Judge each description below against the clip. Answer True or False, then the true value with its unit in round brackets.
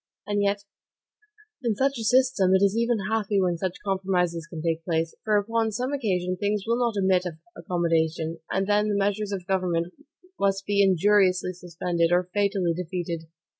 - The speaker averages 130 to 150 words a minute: False (170 wpm)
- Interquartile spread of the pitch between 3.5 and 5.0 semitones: False (2.8 semitones)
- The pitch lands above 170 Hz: True (190 Hz)